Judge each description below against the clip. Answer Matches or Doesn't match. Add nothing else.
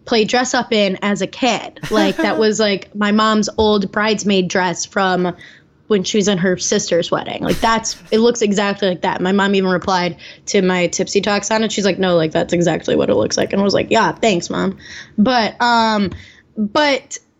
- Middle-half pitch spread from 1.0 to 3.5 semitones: Matches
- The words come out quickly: Matches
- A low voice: Doesn't match